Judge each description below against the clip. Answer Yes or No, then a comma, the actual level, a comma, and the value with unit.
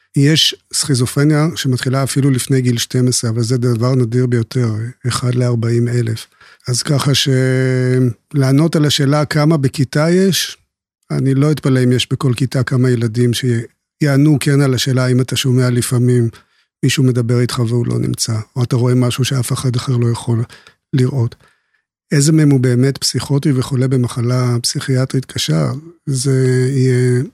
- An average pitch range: No, narrow, 2.1 semitones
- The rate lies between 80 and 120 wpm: No, average, 145 wpm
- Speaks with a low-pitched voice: Yes, low, 130 Hz